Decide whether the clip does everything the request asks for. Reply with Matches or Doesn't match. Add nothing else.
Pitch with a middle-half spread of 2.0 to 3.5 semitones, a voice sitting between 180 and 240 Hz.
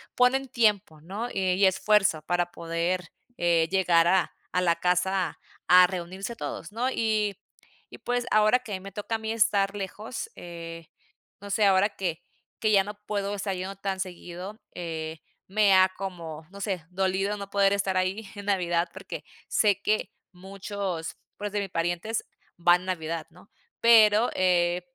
Matches